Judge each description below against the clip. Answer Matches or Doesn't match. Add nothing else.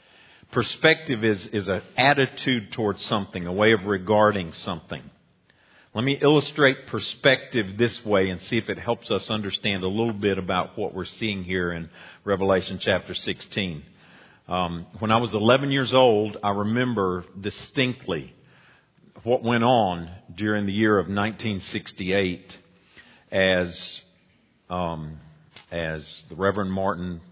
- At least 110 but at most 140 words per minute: Matches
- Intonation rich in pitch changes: Doesn't match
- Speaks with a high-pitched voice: Doesn't match